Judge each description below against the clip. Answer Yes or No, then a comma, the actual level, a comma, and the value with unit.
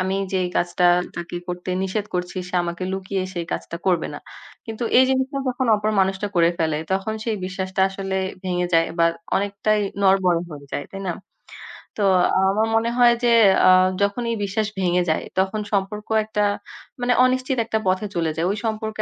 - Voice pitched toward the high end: Yes, high, 195 Hz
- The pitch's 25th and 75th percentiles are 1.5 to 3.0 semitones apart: No, average, 3.4 semitones